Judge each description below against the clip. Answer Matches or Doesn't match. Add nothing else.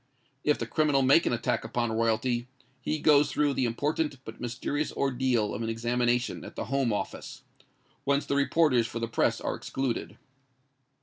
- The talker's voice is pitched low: Matches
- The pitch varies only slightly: Doesn't match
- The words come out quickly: Doesn't match